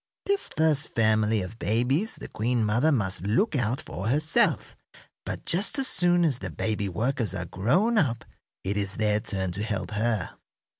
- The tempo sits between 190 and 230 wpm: No, average, 170 wpm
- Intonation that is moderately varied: No, wide, 6.4 semitones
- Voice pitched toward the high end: No, low, 115 Hz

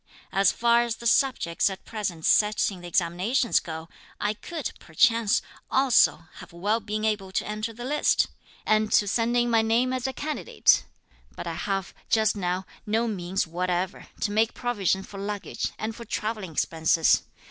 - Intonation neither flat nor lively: Yes, average, 4.0 semitones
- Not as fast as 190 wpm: Yes, average, 170 wpm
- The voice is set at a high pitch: Yes, high, 210 Hz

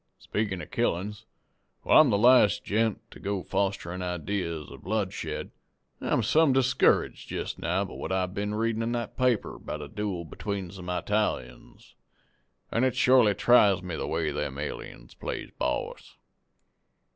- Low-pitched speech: Yes, low, 100 Hz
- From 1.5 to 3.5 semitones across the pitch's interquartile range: No, average, 3.9 semitones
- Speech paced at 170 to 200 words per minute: No, average, 155 wpm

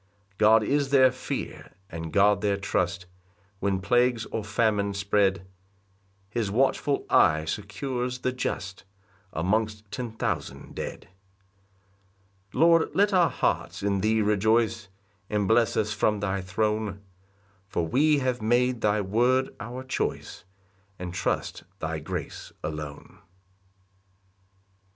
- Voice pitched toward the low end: Yes, low, 105 Hz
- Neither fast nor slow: No, slow, 125 wpm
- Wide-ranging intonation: No, average, 3.9 semitones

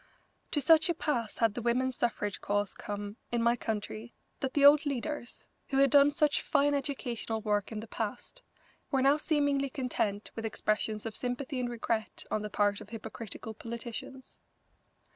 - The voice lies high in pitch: Yes, high, 240 Hz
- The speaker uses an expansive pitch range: No, average, 4.3 semitones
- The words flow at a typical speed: Yes, average, 170 wpm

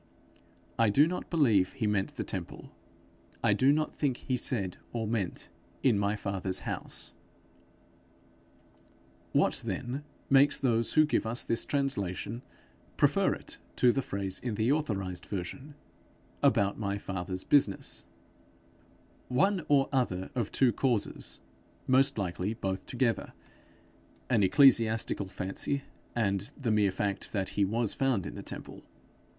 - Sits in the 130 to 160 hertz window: No, low, 115 Hz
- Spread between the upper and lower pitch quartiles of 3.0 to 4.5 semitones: No, average, 5.3 semitones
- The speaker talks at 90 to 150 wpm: Yes, slow, 135 wpm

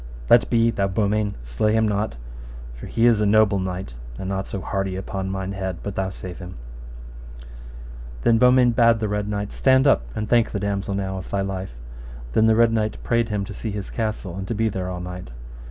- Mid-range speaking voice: No, low, 100 Hz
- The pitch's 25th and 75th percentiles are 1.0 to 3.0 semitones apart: Yes, average, 2.7 semitones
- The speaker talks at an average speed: No, fast, 215 wpm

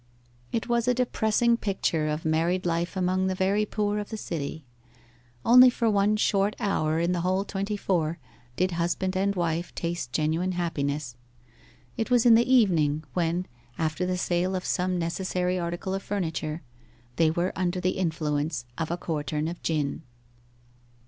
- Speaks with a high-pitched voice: No, medium, 180 Hz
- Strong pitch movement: No, average, 3.5 semitones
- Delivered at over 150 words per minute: Yes, average, 160 wpm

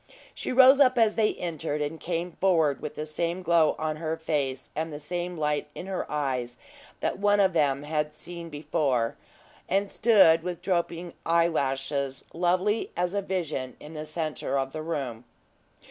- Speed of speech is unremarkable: Yes, average, 170 wpm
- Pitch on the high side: No, medium, 160 Hz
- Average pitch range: Yes, average, 3.3 semitones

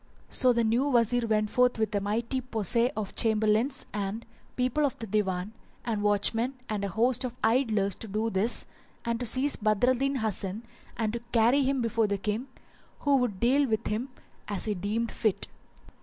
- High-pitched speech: Yes, high, 225 Hz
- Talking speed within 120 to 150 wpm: No, average, 185 wpm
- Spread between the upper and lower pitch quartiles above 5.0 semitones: No, average, 2.9 semitones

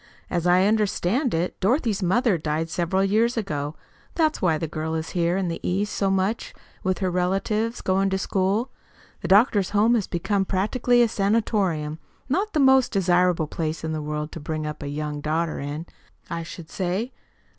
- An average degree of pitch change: Yes, average, 4.7 semitones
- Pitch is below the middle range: No, medium, 185 Hz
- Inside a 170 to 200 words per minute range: Yes, average, 180 wpm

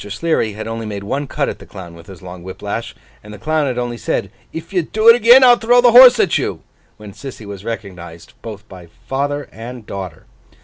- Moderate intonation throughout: No, wide, 8.4 semitones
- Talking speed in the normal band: No, fast, 225 wpm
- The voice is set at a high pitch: No, low, 115 Hz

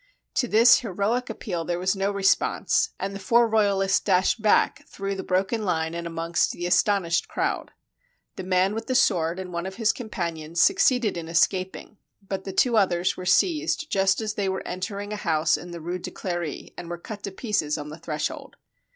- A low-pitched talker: No, high, 190 Hz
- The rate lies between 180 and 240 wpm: Yes, average, 200 wpm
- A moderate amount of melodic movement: Yes, average, 3.3 semitones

